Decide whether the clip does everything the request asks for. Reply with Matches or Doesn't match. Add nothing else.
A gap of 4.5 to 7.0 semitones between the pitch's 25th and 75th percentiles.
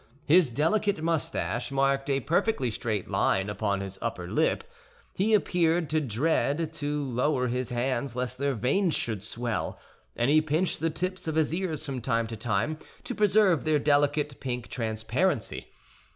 Matches